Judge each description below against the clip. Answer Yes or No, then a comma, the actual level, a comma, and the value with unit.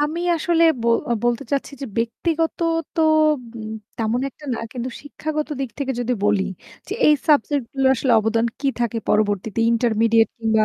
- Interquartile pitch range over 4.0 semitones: Yes, average, 4.5 semitones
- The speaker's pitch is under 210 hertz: No, high, 240 Hz